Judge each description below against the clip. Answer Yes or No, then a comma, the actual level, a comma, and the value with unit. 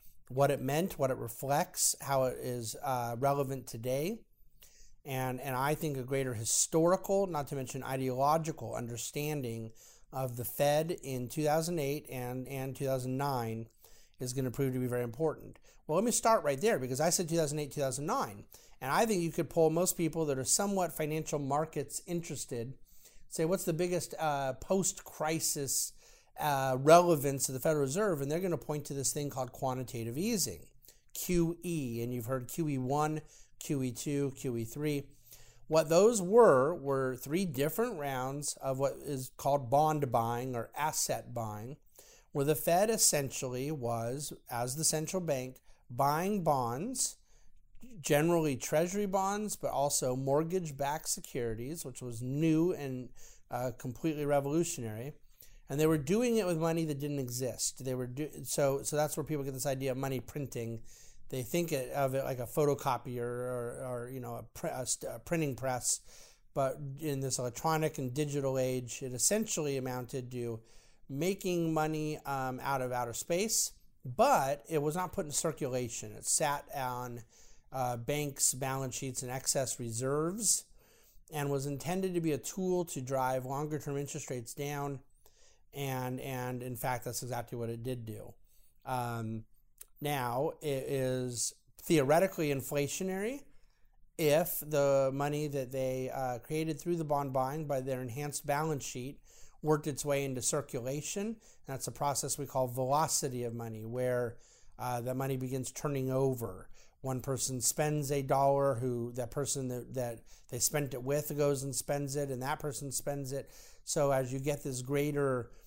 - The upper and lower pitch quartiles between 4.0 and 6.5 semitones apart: No, average, 3.2 semitones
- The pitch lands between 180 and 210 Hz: No, medium, 140 Hz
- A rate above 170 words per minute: No, average, 165 wpm